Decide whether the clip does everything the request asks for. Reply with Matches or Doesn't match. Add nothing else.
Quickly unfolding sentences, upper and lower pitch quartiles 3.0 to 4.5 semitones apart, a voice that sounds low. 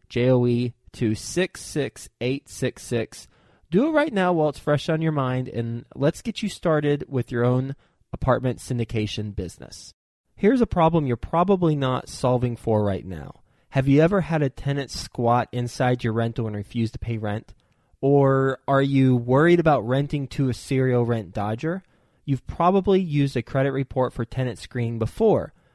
Doesn't match